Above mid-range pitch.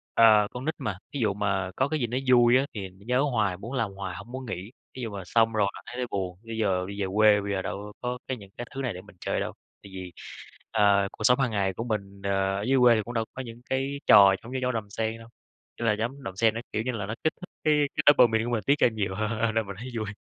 No: low, 110 Hz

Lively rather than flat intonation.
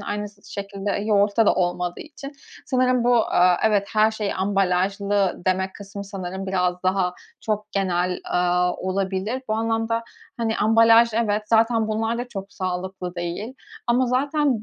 No: average, 3.2 semitones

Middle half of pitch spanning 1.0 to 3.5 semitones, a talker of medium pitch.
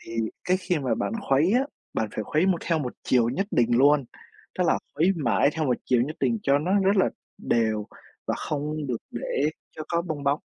No: wide, 5.4 semitones; medium, 145 Hz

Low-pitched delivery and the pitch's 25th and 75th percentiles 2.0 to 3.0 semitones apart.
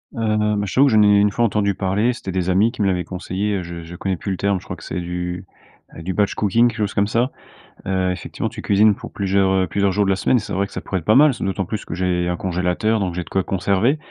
Yes: low, 100 Hz; narrow, 2.6 semitones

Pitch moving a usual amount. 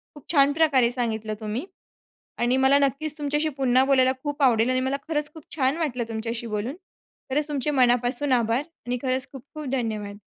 Yes: average, 3.4 semitones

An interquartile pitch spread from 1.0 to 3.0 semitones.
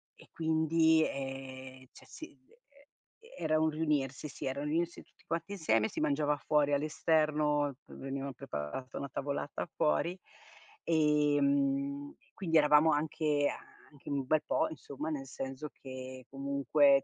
Yes: narrow, 2.5 semitones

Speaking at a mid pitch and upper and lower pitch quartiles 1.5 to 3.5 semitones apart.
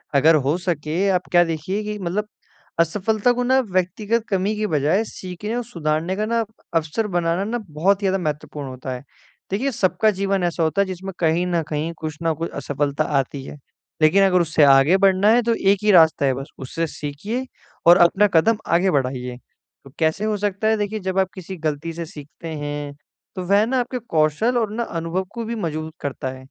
No: medium, 175 Hz; average, 5.1 semitones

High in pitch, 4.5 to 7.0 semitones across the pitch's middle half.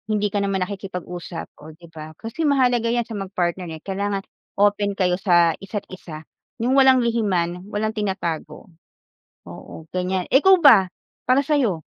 No: high, 195 Hz; average, 4.1 semitones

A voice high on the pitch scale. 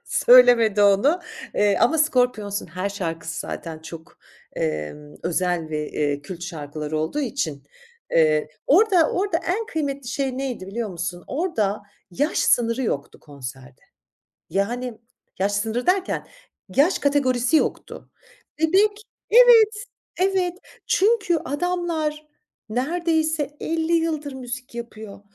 Yes: high, 245 Hz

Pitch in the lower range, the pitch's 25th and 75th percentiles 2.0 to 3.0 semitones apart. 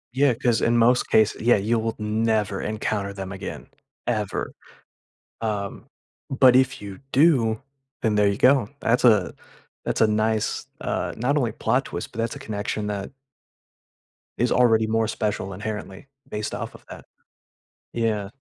Yes: low, 110 Hz; narrow, 2.6 semitones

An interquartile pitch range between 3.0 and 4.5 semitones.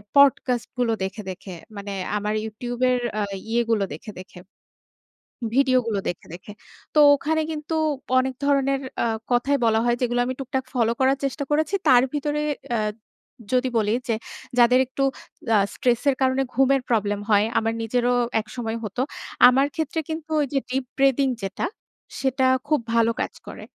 Yes: average, 3.4 semitones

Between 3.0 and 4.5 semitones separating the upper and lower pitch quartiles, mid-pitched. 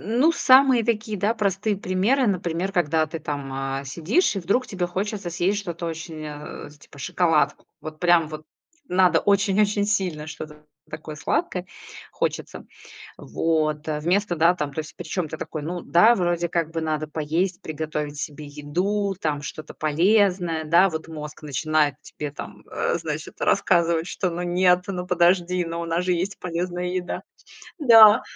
Yes: average, 3.7 semitones; medium, 175 Hz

